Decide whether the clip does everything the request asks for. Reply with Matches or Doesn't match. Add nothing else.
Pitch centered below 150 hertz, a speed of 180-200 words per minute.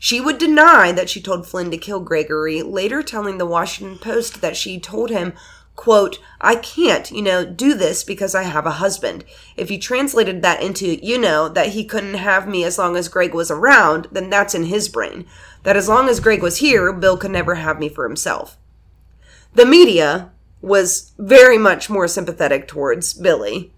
Doesn't match